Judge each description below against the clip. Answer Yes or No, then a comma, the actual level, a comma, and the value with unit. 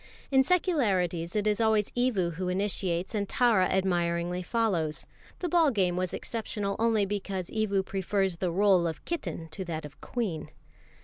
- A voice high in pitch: Yes, high, 195 Hz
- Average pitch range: Yes, average, 3.9 semitones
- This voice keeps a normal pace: Yes, average, 160 wpm